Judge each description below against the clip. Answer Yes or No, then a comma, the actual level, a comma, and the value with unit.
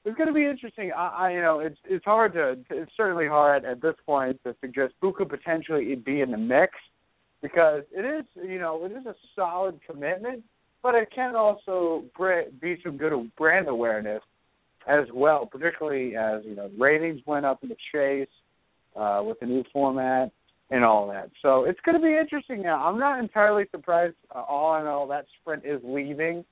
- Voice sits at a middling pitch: Yes, medium, 160 Hz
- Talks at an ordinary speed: Yes, average, 195 wpm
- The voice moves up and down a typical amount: No, wide, 6.1 semitones